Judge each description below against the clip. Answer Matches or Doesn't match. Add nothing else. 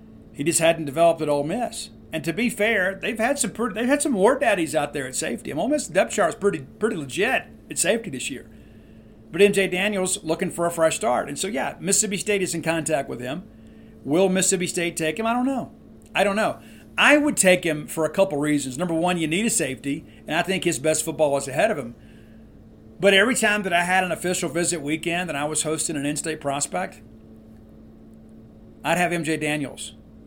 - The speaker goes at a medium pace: Doesn't match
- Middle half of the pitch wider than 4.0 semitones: Matches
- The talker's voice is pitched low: Doesn't match